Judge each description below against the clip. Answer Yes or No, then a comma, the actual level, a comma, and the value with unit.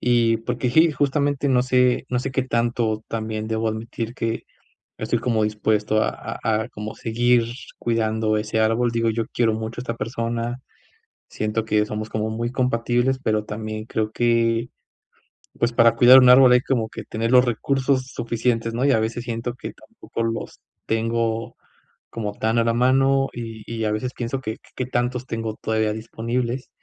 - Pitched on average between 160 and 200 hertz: No, low, 115 Hz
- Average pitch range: No, narrow, 2.0 semitones